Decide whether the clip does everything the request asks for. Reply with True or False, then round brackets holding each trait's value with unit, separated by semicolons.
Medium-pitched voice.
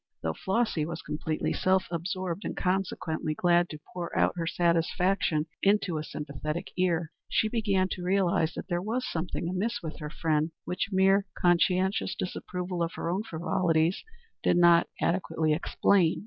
True (175 Hz)